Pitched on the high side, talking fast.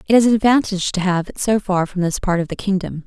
Yes: high, 195 Hz; fast, 295 wpm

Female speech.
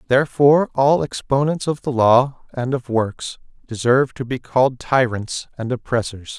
No: male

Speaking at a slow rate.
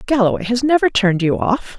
No: average, 200 wpm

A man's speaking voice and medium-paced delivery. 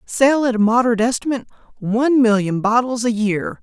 No: female; average, 165 wpm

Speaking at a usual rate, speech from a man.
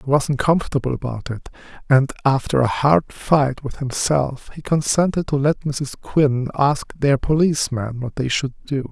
Yes: average, 175 wpm; male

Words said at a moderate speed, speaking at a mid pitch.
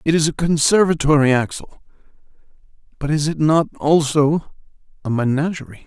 No: slow, 125 wpm; medium, 150 Hz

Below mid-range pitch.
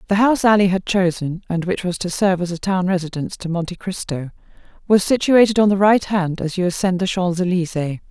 No: medium, 185 Hz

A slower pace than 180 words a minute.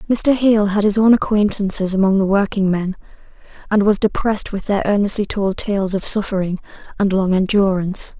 Yes: average, 170 wpm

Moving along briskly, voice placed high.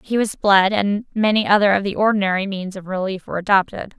Yes: fast, 210 wpm; high, 200 Hz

